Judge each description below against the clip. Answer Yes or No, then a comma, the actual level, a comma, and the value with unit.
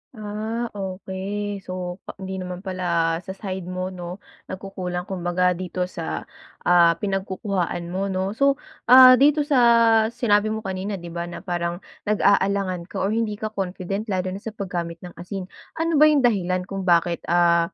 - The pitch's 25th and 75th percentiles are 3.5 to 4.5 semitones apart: No, average, 2.9 semitones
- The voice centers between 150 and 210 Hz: Yes, high, 190 Hz